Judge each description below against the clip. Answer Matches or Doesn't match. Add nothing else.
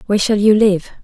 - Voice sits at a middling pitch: Doesn't match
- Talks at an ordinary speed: Doesn't match